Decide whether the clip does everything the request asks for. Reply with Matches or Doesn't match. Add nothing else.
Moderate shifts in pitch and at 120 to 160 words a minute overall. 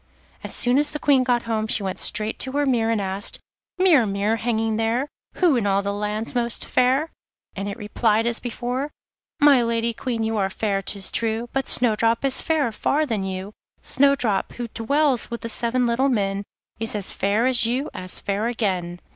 Doesn't match